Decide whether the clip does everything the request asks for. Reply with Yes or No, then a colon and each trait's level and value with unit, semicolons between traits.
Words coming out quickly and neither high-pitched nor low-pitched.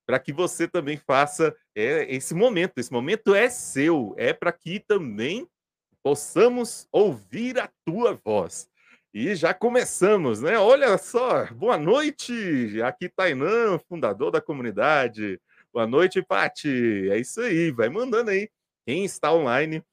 No: average, 140 wpm; medium, 180 Hz